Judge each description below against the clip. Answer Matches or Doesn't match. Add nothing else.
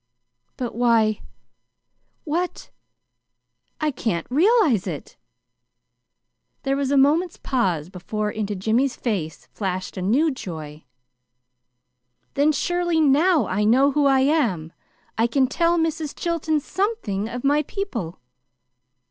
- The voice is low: Doesn't match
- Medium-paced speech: Doesn't match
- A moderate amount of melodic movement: Doesn't match